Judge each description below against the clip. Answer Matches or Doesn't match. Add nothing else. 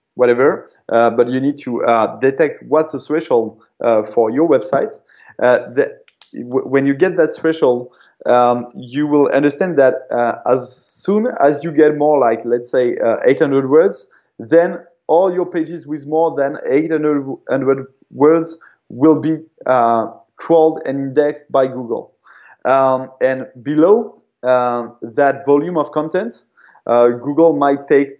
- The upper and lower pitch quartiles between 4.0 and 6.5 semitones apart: Doesn't match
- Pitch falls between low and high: Matches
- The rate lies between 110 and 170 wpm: Matches